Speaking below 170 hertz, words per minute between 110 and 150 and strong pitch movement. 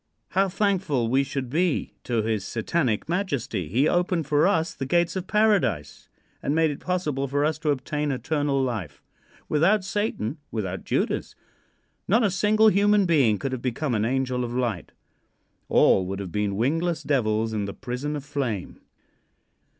No: medium, 140 Hz; average, 165 wpm; wide, 6.8 semitones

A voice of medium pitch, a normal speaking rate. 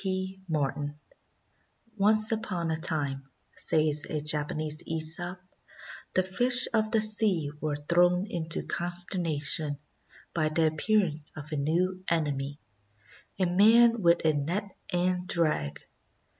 No: medium, 170 Hz; slow, 130 wpm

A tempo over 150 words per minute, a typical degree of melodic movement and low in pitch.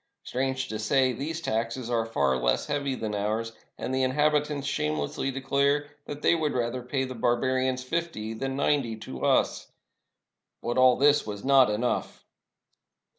Yes: average, 160 wpm; average, 3.6 semitones; low, 130 Hz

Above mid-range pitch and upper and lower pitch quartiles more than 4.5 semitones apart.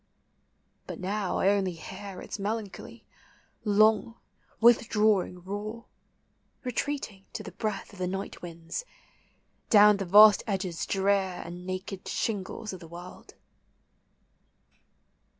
No: high, 195 Hz; narrow, 2.5 semitones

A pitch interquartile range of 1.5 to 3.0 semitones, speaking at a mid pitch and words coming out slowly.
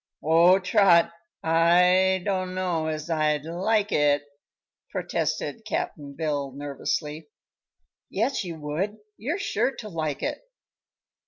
No: average, 3.7 semitones; medium, 170 Hz; slow, 105 wpm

